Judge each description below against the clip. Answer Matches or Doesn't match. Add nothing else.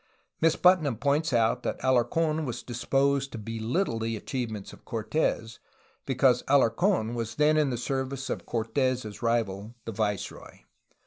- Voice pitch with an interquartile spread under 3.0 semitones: Doesn't match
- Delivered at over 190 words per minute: Doesn't match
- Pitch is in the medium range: Doesn't match